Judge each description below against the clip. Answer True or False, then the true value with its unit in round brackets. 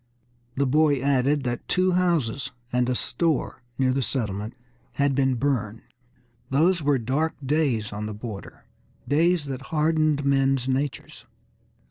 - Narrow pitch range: False (3.5 semitones)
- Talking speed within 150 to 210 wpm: False (135 wpm)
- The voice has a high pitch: False (135 Hz)